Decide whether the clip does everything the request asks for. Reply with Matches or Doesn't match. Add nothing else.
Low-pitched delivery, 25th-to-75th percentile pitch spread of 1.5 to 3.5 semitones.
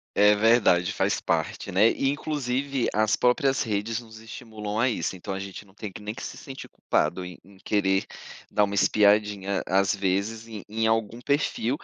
Matches